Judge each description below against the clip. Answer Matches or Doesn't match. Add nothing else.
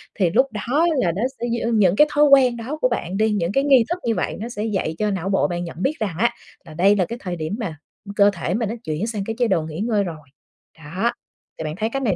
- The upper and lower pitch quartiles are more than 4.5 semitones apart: Matches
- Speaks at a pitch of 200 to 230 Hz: Matches